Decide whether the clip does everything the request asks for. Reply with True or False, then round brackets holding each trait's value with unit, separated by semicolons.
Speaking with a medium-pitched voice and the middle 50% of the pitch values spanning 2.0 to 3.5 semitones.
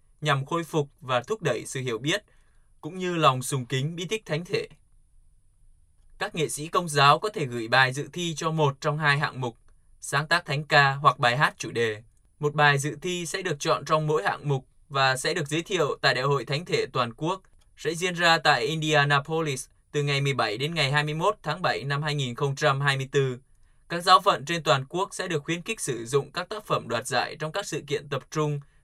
True (150 Hz; 3.1 semitones)